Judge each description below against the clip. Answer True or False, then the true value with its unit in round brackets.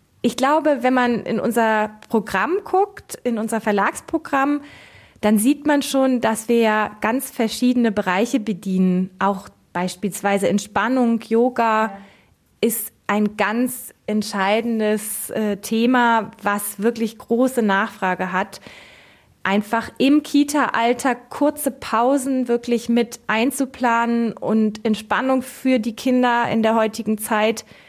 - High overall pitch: True (230 Hz)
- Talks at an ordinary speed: False (110 wpm)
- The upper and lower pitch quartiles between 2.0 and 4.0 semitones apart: True (3.1 semitones)